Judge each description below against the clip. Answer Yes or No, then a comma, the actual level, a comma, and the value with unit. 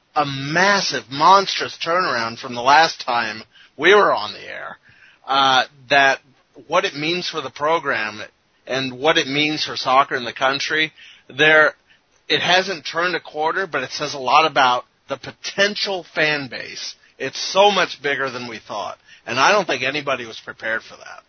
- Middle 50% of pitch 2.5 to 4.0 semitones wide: Yes, average, 3.6 semitones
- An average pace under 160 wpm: No, average, 175 wpm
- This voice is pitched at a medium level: Yes, medium, 150 Hz